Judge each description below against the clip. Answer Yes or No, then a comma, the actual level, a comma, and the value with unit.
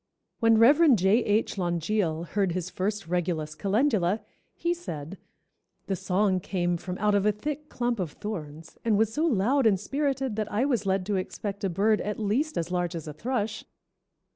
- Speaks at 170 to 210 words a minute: Yes, average, 185 wpm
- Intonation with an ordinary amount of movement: Yes, average, 4.2 semitones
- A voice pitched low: No, high, 205 Hz